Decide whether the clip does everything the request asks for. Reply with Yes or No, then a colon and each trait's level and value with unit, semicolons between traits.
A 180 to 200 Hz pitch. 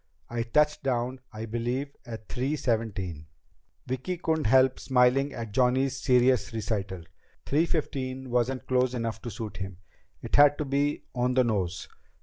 No: low, 125 Hz